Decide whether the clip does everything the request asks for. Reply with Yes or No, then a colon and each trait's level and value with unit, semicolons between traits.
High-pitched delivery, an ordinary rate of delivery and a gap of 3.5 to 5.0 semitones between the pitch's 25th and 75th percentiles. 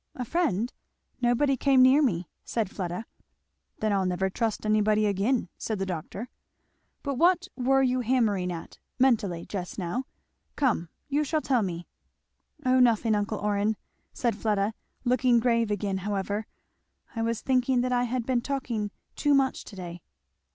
Yes: high, 225 Hz; average, 155 wpm; average, 4.2 semitones